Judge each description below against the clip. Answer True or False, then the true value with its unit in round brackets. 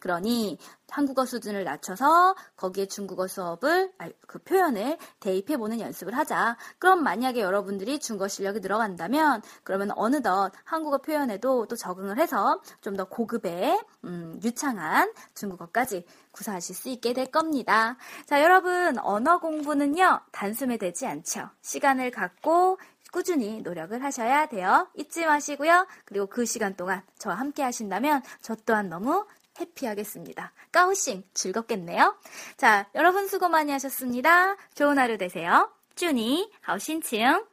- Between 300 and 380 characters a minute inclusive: True (325 characters per minute)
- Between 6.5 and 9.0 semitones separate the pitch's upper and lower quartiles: True (7.8 semitones)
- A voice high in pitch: True (260 Hz)